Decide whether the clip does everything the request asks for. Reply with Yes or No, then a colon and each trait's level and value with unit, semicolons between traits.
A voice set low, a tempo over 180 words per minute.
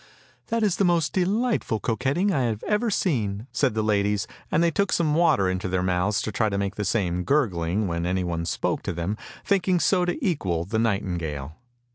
Yes: low, 110 Hz; fast, 205 wpm